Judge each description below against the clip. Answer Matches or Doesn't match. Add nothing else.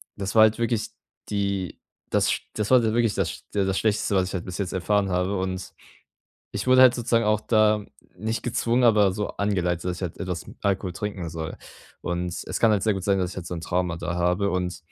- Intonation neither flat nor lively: Matches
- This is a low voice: Matches